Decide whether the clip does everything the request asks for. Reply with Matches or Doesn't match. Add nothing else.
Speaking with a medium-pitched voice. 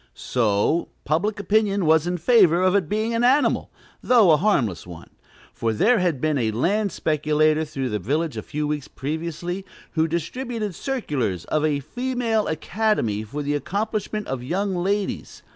Matches